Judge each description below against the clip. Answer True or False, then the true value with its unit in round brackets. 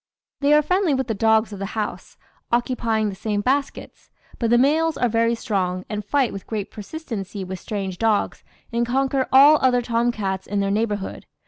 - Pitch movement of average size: True (4.3 semitones)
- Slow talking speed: False (190 wpm)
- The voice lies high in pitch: True (225 Hz)